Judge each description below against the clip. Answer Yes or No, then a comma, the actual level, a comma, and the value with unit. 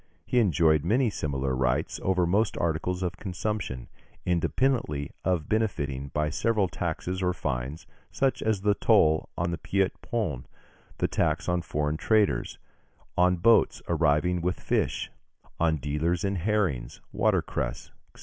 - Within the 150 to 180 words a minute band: No, average, 140 wpm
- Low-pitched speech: Yes, very low, 85 Hz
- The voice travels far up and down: No, average, 4.8 semitones